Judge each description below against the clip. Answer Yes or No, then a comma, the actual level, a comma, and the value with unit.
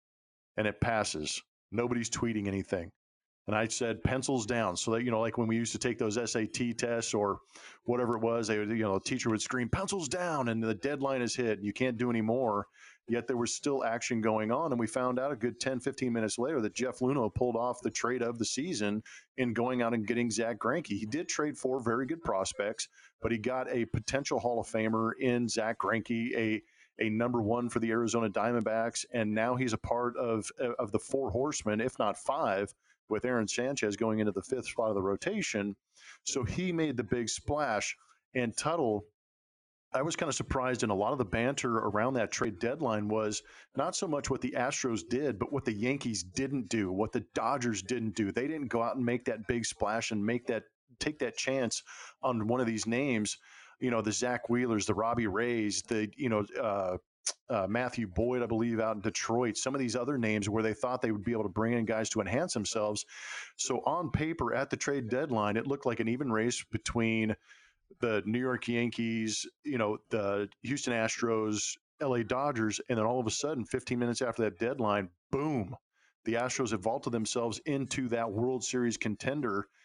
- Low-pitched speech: Yes, low, 115 Hz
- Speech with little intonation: Yes, narrow, 2.3 semitones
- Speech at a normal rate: No, fast, 210 wpm